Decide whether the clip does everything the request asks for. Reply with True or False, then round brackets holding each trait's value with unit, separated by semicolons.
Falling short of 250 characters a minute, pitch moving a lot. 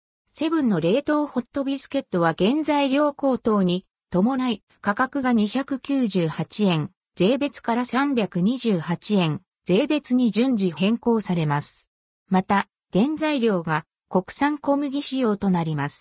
True (225 characters per minute; 7.1 semitones)